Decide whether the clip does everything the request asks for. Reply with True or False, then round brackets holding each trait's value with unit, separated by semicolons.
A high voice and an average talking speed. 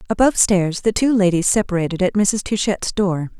True (195 Hz; 175 wpm)